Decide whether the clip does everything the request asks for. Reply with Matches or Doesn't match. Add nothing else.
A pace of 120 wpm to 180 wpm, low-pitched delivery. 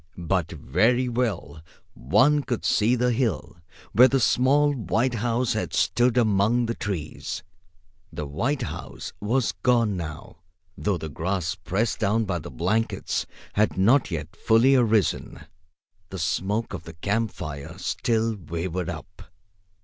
Matches